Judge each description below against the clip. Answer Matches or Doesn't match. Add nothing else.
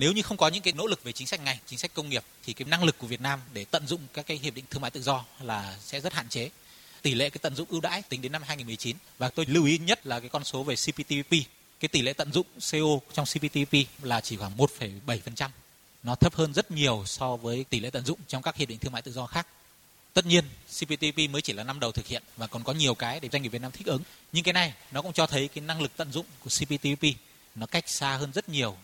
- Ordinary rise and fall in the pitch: Matches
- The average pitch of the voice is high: Doesn't match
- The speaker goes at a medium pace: Doesn't match